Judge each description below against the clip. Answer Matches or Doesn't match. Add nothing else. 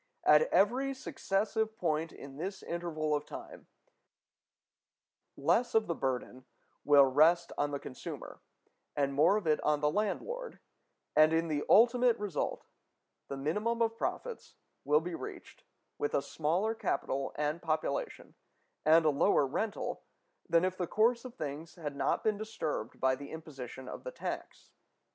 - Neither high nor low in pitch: Matches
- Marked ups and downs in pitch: Matches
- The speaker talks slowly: Doesn't match